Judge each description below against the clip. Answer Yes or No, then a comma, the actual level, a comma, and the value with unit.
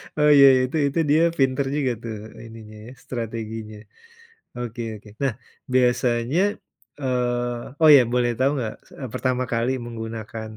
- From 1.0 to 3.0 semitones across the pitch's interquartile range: Yes, narrow, 2.4 semitones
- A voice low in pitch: Yes, low, 120 Hz